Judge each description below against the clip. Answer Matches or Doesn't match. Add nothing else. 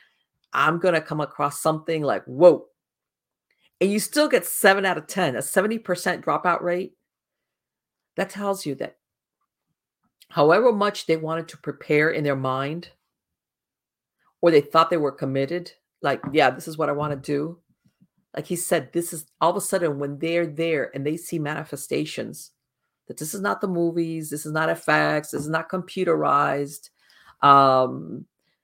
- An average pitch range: Matches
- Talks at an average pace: Matches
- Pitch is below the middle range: Doesn't match